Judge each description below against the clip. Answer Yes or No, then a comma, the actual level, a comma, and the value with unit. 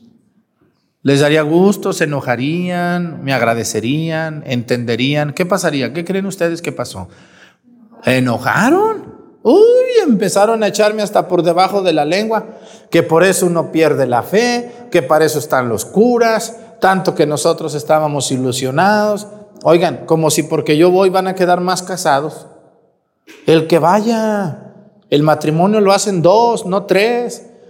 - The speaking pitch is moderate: Yes, medium, 180 Hz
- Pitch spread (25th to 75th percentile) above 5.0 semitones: Yes, wide, 5.4 semitones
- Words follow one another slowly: No, average, 140 wpm